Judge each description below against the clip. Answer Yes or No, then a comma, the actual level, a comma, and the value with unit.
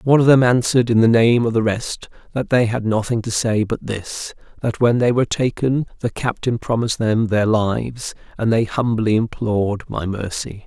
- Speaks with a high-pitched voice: No, low, 115 Hz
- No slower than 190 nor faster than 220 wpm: Yes, average, 195 wpm